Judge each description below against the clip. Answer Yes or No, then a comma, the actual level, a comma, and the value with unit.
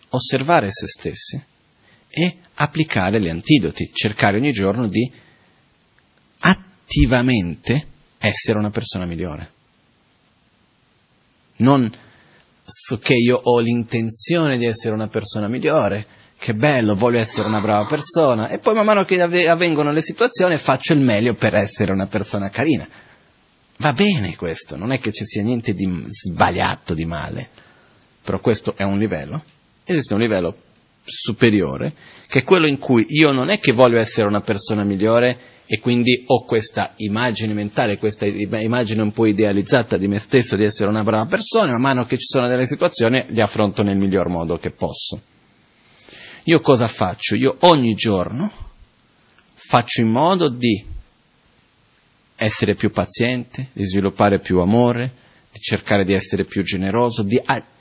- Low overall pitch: Yes, low, 115 Hz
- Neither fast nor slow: Yes, average, 150 wpm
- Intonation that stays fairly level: No, average, 4.2 semitones